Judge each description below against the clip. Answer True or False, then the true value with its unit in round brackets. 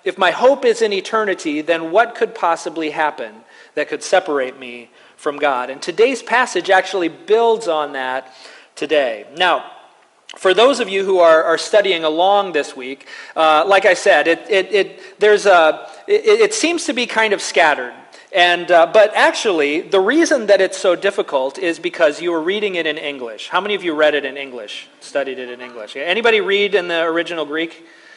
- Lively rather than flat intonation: True (6.1 semitones)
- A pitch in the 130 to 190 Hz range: True (185 Hz)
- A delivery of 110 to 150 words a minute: False (195 wpm)